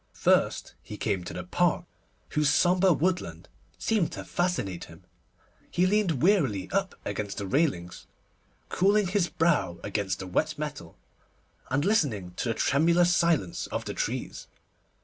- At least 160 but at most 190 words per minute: No, average, 145 wpm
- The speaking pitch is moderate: Yes, medium, 155 Hz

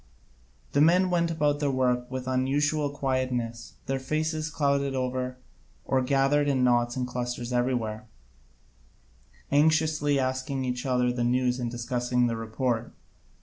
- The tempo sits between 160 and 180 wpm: No, average, 140 wpm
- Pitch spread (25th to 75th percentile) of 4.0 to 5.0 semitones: No, narrow, 2.6 semitones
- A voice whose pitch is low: Yes, low, 130 Hz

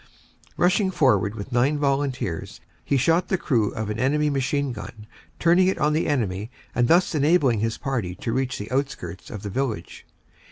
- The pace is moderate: Yes, average, 175 wpm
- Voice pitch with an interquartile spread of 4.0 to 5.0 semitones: No, wide, 5.6 semitones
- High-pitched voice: No, low, 130 Hz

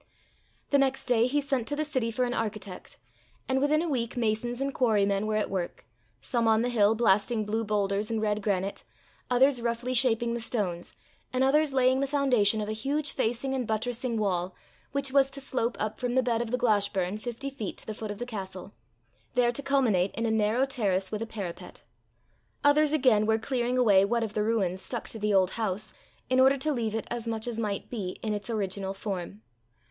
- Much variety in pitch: No, average, 3.5 semitones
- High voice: Yes, high, 230 Hz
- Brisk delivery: Yes, fast, 210 wpm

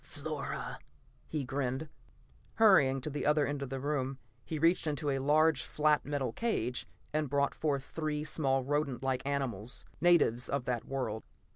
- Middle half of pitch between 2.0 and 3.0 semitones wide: Yes, narrow, 2.5 semitones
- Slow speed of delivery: No, average, 160 wpm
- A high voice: No, medium, 140 Hz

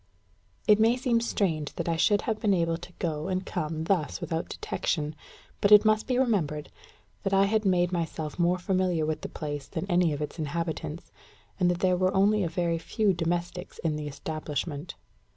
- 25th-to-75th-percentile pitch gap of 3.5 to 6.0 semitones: Yes, average, 3.8 semitones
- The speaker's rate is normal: Yes, average, 190 wpm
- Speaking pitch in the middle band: Yes, medium, 175 Hz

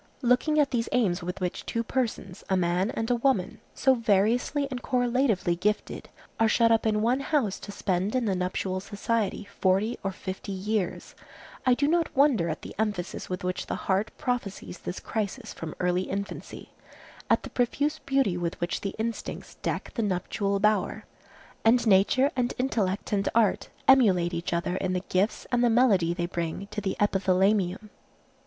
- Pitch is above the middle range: Yes, high, 205 Hz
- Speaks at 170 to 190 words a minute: Yes, average, 175 wpm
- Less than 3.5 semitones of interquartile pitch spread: No, average, 4.5 semitones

